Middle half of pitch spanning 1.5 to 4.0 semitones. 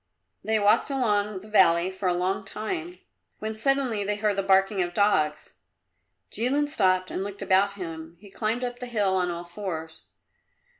Yes: average, 2.8 semitones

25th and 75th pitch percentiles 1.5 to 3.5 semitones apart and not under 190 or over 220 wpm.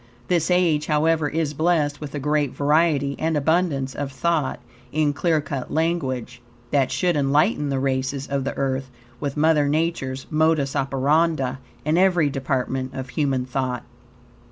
No: average, 3.0 semitones; average, 150 wpm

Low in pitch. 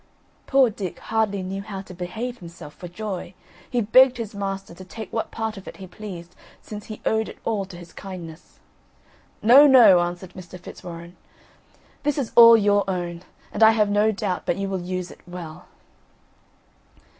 No: high, 195 Hz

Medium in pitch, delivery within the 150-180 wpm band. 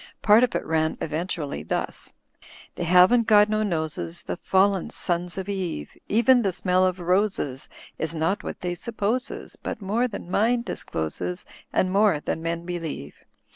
Yes: medium, 180 Hz; average, 165 wpm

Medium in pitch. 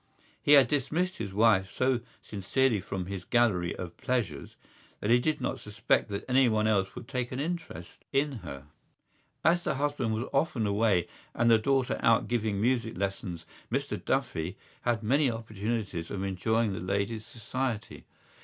No: low, 115 Hz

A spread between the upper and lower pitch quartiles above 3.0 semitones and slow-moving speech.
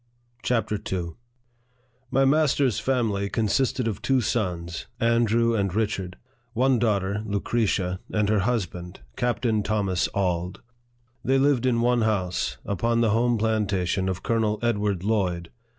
Yes: average, 3.5 semitones; slow, 130 wpm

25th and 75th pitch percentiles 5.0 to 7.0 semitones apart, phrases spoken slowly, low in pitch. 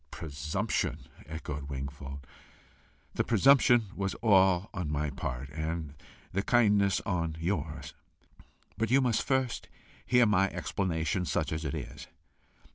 Yes: wide, 5.6 semitones; slow, 120 wpm; very low, 90 Hz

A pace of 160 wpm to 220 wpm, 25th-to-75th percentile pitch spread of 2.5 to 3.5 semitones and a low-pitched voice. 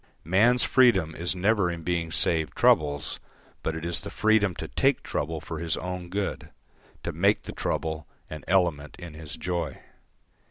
Yes: average, 165 wpm; average, 2.9 semitones; very low, 85 Hz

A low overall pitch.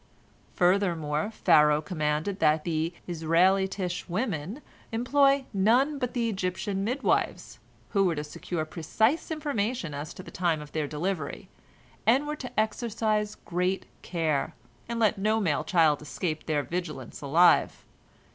No: medium, 185 Hz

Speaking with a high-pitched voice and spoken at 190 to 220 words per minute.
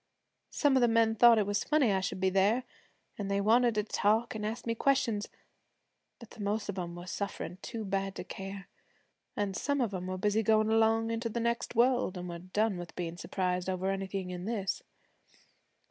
Yes: high, 205 Hz; fast, 205 wpm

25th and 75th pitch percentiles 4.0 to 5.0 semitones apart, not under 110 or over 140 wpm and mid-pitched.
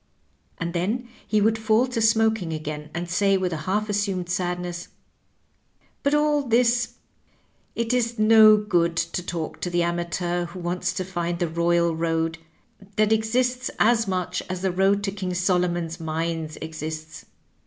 No: average, 4.3 semitones; average, 160 wpm; medium, 180 Hz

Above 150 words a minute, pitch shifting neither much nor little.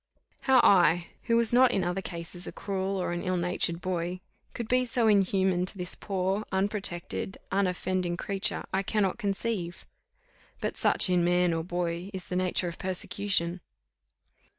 No: average, 160 wpm; narrow, 2.1 semitones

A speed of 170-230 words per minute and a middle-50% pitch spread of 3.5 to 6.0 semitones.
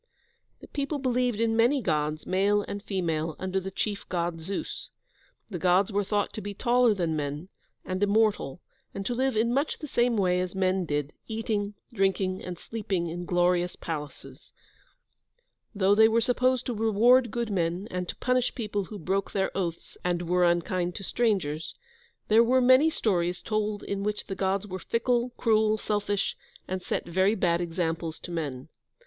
Yes: average, 175 wpm; average, 4.1 semitones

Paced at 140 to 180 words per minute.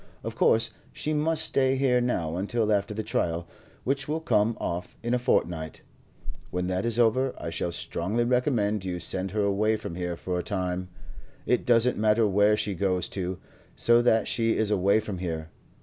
No: average, 190 wpm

